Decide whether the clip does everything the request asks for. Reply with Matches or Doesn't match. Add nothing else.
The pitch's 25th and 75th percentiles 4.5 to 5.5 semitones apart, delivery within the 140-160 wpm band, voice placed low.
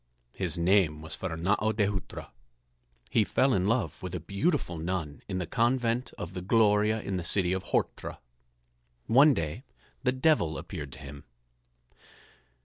Matches